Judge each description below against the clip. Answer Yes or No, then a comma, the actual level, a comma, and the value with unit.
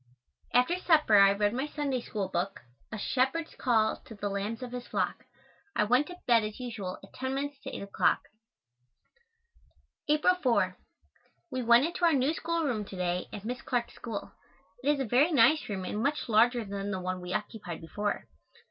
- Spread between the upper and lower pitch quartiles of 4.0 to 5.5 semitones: Yes, average, 5.2 semitones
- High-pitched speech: Yes, high, 235 Hz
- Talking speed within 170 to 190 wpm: Yes, average, 185 wpm